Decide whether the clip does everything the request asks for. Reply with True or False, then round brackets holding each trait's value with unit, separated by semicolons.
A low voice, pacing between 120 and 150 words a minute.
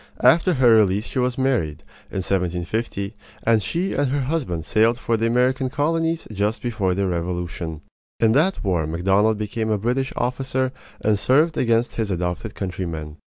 False (110 Hz; 160 wpm)